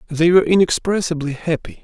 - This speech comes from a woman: No, male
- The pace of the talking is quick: No, slow, 130 wpm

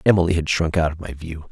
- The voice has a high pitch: No, very low, 80 Hz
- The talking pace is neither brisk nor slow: No, fast, 275 wpm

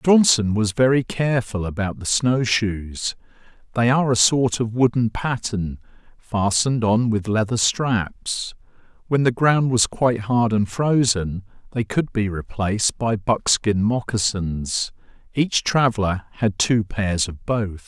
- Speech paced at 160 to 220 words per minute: No, average, 140 wpm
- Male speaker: Yes, male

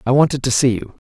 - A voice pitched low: Yes, low, 130 Hz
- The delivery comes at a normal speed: No, fast, 280 wpm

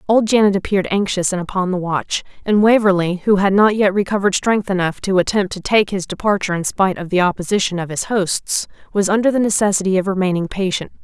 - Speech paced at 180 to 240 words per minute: Yes, fast, 205 wpm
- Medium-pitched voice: No, high, 195 Hz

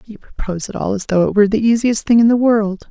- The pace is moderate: No, fast, 290 wpm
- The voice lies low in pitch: No, high, 215 Hz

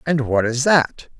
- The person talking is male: Yes, male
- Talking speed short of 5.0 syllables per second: Yes, 4.0 syllables/s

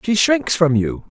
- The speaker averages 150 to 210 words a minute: Yes, fast, 205 wpm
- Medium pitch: Yes, medium, 170 Hz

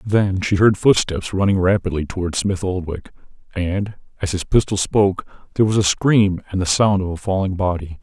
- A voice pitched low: Yes, very low, 95 Hz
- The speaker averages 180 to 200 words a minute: Yes, average, 185 wpm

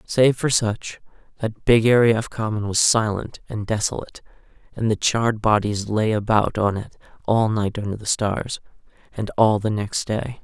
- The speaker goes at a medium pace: Yes, average, 175 wpm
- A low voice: Yes, low, 110 Hz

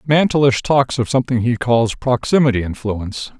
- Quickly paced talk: No, average, 140 wpm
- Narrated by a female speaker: No, male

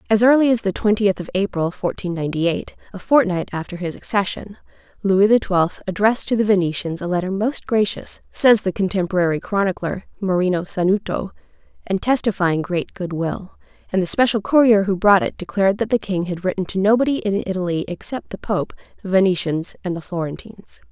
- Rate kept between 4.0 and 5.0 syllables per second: No, 5.7 syllables/s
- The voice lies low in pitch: No, high, 195 Hz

